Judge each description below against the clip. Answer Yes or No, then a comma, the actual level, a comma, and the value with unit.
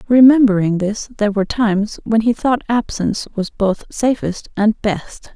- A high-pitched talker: Yes, high, 215 Hz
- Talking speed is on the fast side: No, average, 155 wpm